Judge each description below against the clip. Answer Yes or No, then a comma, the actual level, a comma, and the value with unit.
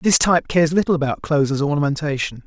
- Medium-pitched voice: Yes, medium, 150 Hz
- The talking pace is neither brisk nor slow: Yes, average, 195 wpm